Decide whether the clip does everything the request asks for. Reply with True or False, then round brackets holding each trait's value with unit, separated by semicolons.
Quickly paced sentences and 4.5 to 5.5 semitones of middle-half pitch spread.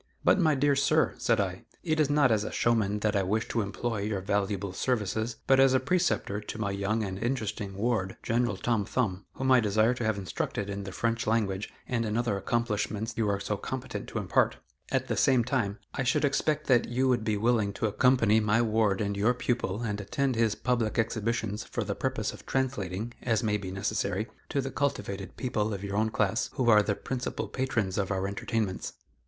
False (210 wpm; 3.5 semitones)